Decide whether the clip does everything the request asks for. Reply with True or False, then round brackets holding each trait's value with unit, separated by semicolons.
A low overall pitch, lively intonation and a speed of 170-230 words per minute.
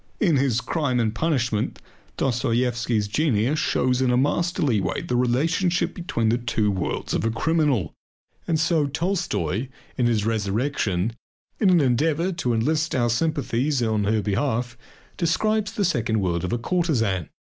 False (125 Hz; 6.0 semitones; 155 wpm)